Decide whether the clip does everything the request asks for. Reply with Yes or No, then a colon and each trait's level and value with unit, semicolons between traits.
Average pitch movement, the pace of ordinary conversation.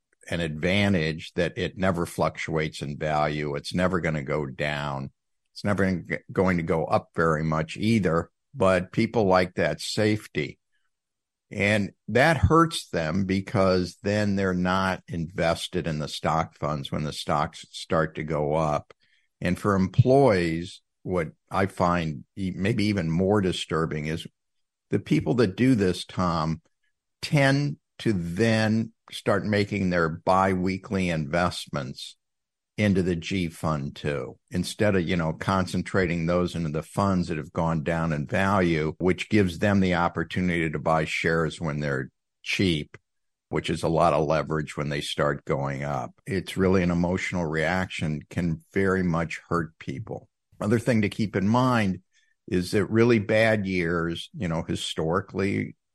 Yes: average, 3.6 semitones; average, 150 wpm